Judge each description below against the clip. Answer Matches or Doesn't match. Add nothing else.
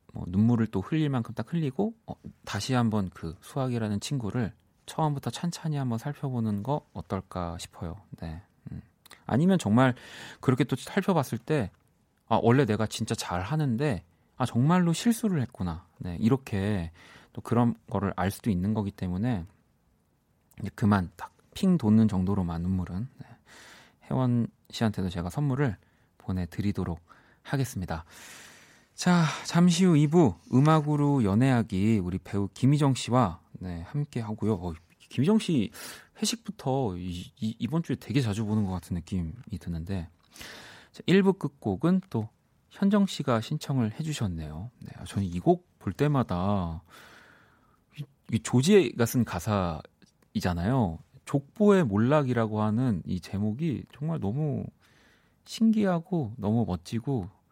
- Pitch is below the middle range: Matches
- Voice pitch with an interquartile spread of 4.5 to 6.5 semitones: Doesn't match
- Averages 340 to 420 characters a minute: Doesn't match